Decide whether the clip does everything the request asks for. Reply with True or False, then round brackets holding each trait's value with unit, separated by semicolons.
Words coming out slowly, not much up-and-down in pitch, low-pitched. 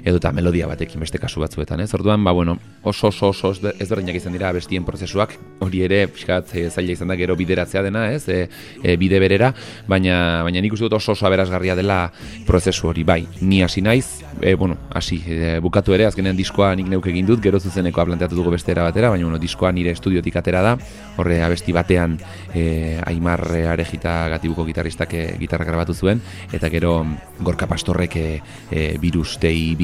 False (190 wpm; 2.3 semitones; 90 Hz)